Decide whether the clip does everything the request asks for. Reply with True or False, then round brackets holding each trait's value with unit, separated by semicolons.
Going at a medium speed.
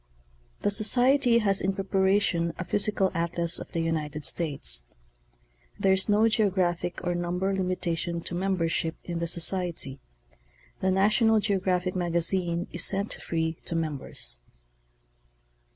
False (125 wpm)